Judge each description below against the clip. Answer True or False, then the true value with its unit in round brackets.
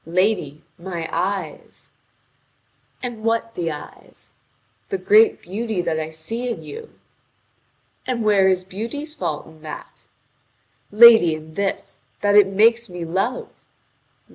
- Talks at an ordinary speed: False (125 wpm)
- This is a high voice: True (195 Hz)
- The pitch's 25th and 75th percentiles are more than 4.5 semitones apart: True (5.4 semitones)